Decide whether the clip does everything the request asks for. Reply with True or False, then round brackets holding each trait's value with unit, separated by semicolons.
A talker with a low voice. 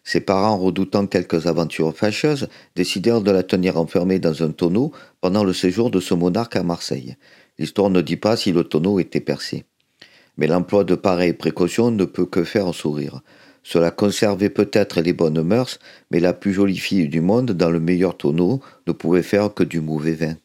True (90 Hz)